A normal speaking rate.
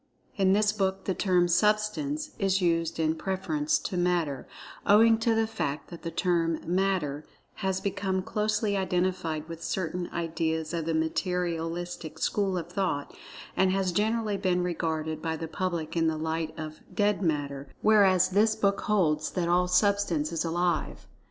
Yes: average, 160 wpm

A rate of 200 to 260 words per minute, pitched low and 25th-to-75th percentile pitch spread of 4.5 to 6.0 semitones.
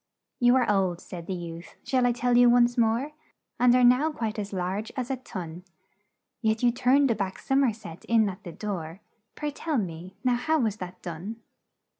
No: fast, 205 wpm; high, 225 Hz; average, 5.0 semitones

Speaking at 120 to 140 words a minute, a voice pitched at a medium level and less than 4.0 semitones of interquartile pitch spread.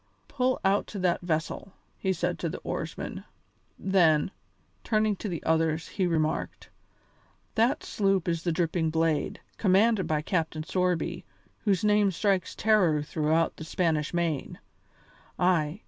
Yes: slow, 135 wpm; medium, 175 Hz; average, 3.4 semitones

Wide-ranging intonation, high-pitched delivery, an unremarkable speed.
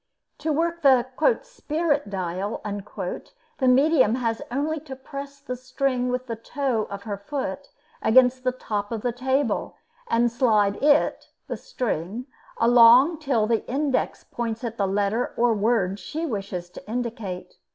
No: average, 4.6 semitones; high, 245 Hz; average, 150 wpm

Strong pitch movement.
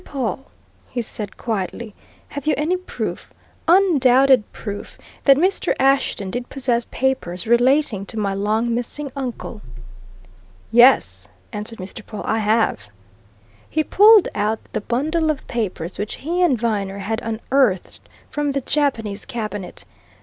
No: average, 4.8 semitones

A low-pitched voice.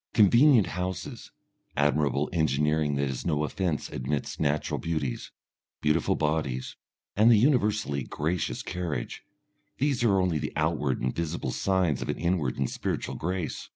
Yes: very low, 80 Hz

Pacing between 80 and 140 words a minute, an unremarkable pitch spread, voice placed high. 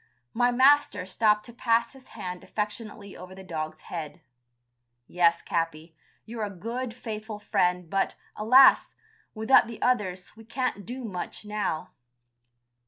Yes: slow, 135 wpm; average, 4.5 semitones; high, 210 Hz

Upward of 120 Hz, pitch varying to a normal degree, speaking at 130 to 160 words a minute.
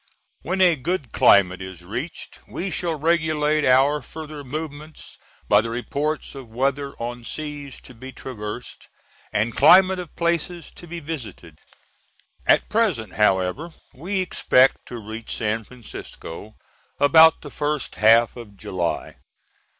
No: medium, 140 Hz; wide, 6.0 semitones; slow, 135 wpm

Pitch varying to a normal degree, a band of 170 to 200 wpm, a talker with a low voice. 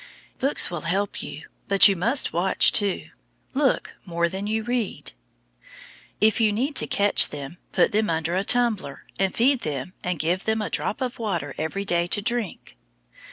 No: average, 4.6 semitones; average, 175 wpm; high, 200 Hz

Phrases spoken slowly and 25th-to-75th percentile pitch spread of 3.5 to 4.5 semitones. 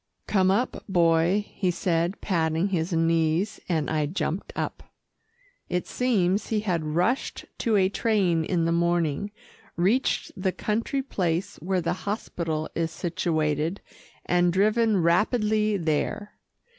Yes: slow, 130 wpm; average, 3.8 semitones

